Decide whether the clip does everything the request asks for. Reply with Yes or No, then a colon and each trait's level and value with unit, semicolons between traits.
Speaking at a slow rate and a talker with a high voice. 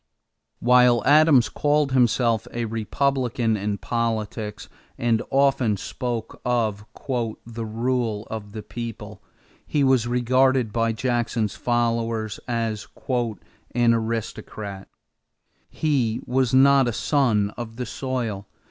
No: slow, 110 wpm; low, 115 Hz